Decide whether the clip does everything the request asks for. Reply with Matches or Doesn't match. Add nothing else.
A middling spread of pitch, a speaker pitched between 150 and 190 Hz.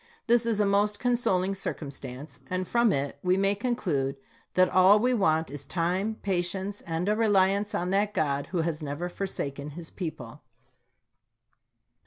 Matches